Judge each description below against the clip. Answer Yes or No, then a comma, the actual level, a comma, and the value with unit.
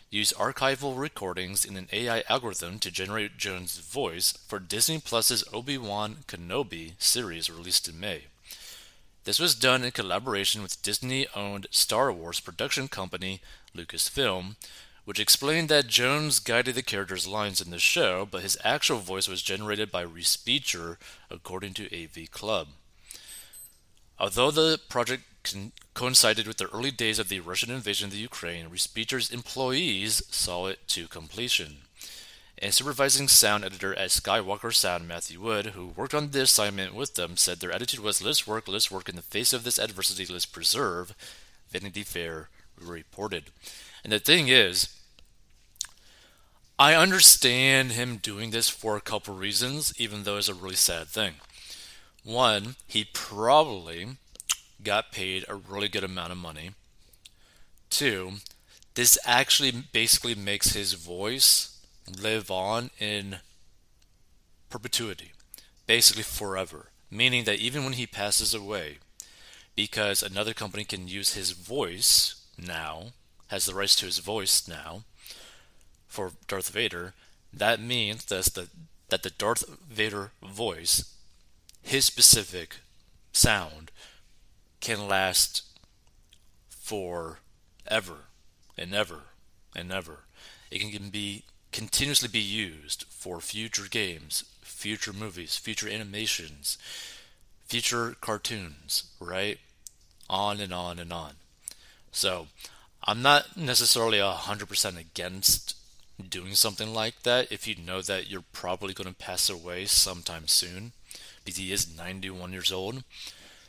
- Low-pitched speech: Yes, low, 100 Hz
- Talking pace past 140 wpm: No, slow, 135 wpm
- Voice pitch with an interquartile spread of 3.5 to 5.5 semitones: Yes, average, 4.0 semitones